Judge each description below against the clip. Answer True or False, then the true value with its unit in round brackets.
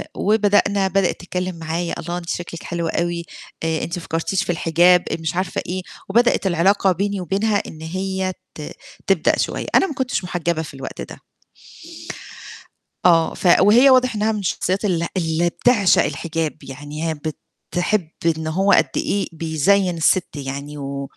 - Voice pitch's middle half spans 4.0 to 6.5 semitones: False (3.3 semitones)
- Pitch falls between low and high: True (175 Hz)